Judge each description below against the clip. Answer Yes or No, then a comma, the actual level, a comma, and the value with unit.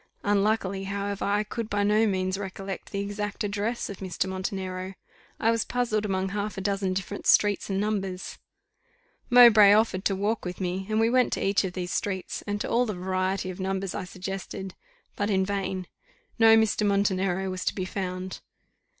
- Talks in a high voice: Yes, high, 195 Hz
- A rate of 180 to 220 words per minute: Yes, average, 185 wpm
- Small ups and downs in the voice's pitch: Yes, narrow, 1.7 semitones